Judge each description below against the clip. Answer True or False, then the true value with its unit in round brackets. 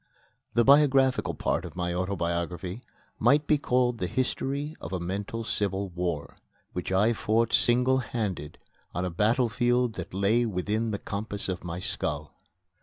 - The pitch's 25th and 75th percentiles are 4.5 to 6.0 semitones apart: True (5.2 semitones)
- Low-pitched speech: True (105 Hz)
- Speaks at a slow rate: False (150 wpm)